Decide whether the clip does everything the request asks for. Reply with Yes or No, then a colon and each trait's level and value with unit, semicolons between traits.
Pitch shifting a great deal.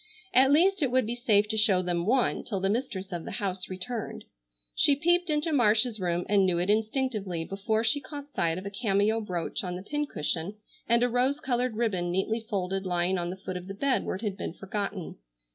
No: average, 4.9 semitones